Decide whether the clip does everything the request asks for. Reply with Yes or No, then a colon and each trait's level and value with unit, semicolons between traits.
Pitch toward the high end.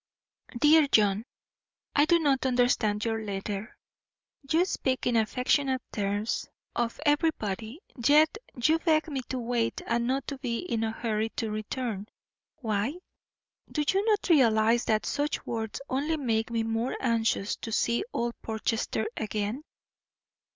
Yes: high, 235 Hz